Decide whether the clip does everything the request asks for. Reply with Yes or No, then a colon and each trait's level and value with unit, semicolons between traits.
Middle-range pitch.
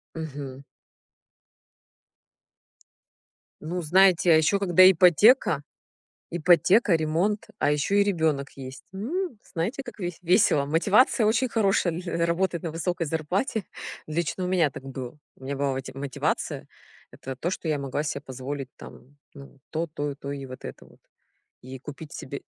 Yes: medium, 160 Hz